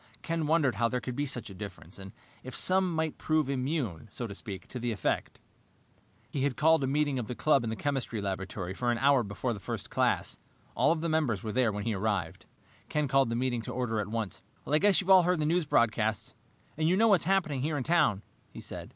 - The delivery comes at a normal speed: No, fast, 235 wpm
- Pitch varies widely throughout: Yes, wide, 5.9 semitones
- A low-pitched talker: Yes, low, 130 Hz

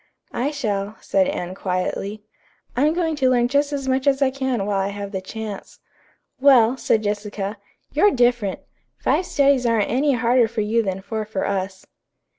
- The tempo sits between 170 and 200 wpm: Yes, average, 175 wpm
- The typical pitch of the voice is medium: No, high, 230 Hz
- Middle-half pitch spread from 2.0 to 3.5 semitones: No, average, 4.9 semitones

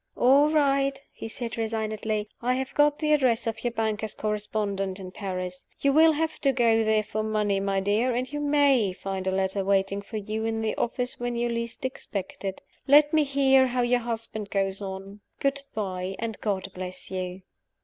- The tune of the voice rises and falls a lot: No, average, 4.6 semitones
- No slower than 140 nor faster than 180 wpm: No, average, 190 wpm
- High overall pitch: Yes, high, 220 Hz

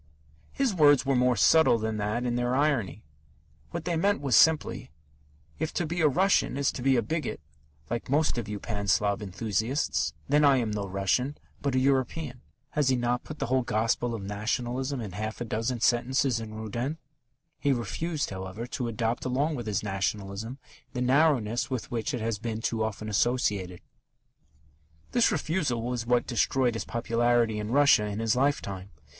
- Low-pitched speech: Yes, low, 120 Hz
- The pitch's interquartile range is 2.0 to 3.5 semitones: No, average, 4.2 semitones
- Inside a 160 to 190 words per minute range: Yes, average, 180 wpm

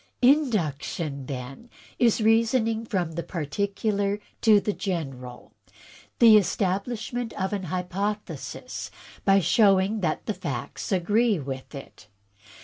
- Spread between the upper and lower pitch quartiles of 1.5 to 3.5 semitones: No, average, 5.2 semitones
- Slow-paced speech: Yes, slow, 110 wpm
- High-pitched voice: Yes, high, 195 Hz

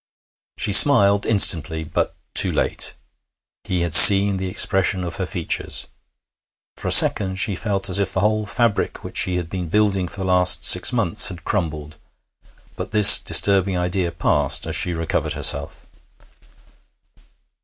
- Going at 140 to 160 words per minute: Yes, average, 155 wpm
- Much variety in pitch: No, narrow, 2.6 semitones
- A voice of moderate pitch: No, very low, 95 Hz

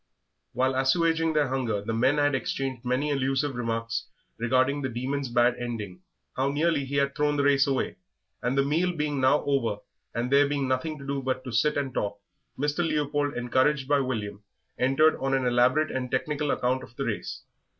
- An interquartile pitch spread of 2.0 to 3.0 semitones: Yes, narrow, 2.5 semitones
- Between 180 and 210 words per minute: Yes, average, 190 wpm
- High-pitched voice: No, low, 135 Hz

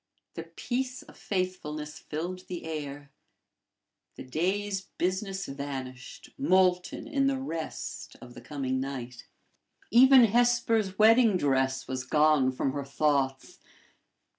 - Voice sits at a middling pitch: Yes, medium, 160 Hz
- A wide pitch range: Yes, wide, 7.0 semitones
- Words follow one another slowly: Yes, slow, 115 wpm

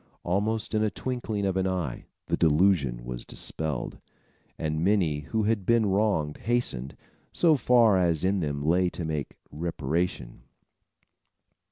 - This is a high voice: No, very low, 90 Hz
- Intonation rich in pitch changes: Yes, wide, 5.8 semitones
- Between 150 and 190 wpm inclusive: No, average, 140 wpm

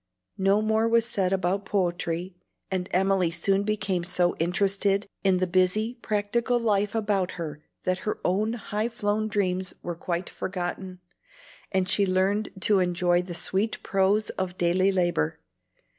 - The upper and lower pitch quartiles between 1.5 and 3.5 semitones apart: Yes, narrow, 2.4 semitones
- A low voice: No, high, 190 Hz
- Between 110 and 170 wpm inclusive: Yes, average, 145 wpm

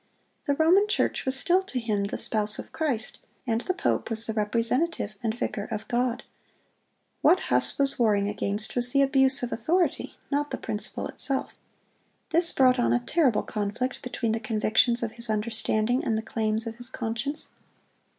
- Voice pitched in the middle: No, high, 240 Hz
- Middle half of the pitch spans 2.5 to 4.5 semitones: Yes, average, 3.8 semitones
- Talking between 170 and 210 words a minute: Yes, average, 175 wpm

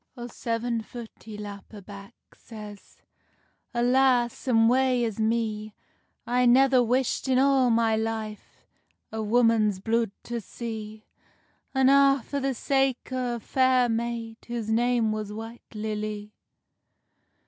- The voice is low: No, high, 230 Hz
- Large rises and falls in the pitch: No, narrow, 2.4 semitones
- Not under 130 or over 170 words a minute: Yes, slow, 135 wpm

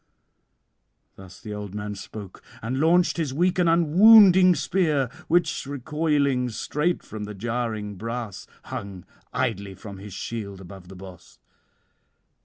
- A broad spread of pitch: Yes, wide, 8.0 semitones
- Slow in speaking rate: Yes, slow, 130 wpm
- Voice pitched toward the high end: No, low, 115 Hz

